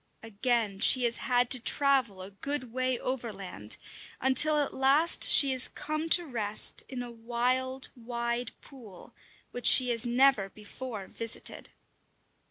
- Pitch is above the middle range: Yes, high, 245 Hz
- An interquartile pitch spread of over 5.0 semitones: No, average, 2.8 semitones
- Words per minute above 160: No, average, 140 wpm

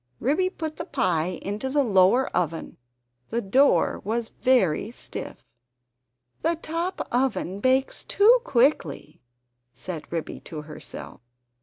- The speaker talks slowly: Yes, slow, 120 wpm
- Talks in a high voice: Yes, high, 240 Hz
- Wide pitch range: Yes, wide, 7.9 semitones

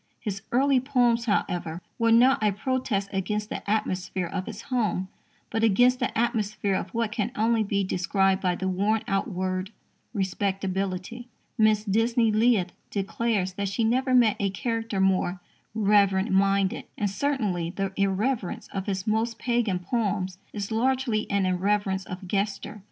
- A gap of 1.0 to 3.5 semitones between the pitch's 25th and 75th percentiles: Yes, average, 3.2 semitones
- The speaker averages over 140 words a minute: Yes, average, 150 wpm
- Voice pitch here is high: Yes, high, 205 Hz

